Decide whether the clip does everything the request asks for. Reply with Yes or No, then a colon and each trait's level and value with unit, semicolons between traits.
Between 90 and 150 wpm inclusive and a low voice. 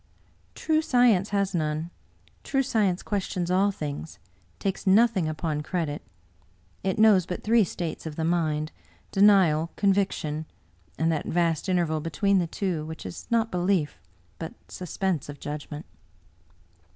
No: average, 140 wpm; medium, 175 Hz